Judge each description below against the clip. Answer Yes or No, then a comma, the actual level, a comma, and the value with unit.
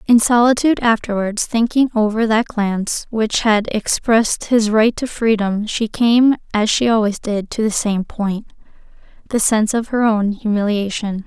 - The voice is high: Yes, high, 220 Hz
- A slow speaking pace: No, average, 155 wpm